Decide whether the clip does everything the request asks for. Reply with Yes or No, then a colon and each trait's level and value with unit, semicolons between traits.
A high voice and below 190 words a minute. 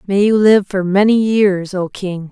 No: high, 195 Hz; fast, 205 wpm